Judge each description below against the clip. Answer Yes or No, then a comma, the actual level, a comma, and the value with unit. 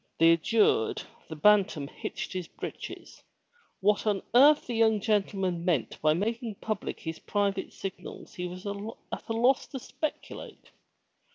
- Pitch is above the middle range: Yes, high, 200 Hz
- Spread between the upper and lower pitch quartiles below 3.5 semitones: No, average, 4.0 semitones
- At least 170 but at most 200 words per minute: No, average, 145 wpm